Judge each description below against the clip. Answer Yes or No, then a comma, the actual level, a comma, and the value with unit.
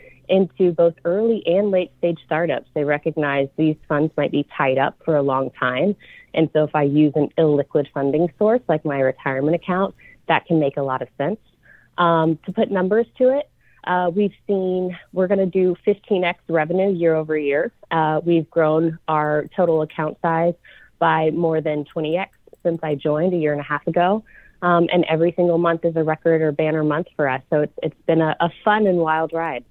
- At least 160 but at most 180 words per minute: No, average, 200 wpm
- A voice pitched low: No, medium, 165 Hz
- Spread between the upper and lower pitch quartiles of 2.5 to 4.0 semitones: Yes, average, 2.8 semitones